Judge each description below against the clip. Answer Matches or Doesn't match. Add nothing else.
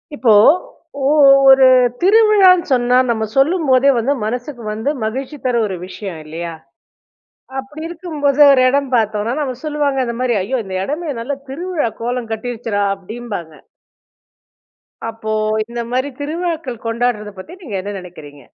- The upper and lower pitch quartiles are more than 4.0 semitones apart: Matches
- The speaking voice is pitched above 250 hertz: Doesn't match